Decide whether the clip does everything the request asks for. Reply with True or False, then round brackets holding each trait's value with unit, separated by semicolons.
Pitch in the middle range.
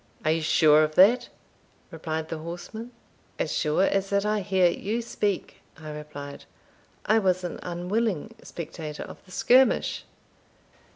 True (180 Hz)